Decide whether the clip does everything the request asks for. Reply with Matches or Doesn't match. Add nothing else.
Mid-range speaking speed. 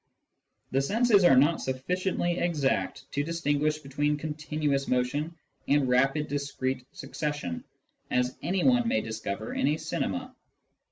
Doesn't match